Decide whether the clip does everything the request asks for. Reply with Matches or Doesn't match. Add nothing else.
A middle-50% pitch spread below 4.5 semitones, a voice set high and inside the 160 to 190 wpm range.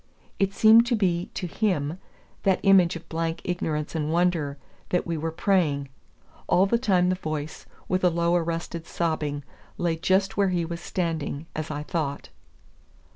Doesn't match